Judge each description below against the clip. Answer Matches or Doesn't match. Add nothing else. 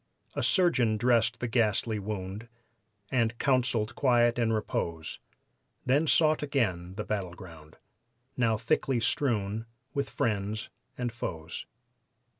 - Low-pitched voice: Matches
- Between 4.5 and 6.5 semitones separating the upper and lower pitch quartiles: Doesn't match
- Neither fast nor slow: Doesn't match